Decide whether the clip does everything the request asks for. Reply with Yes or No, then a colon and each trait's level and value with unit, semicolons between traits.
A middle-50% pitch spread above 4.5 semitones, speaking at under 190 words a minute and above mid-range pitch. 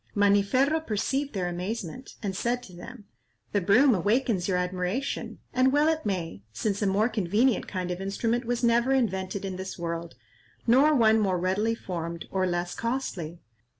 Yes: average, 4.9 semitones; average, 160 wpm; high, 205 Hz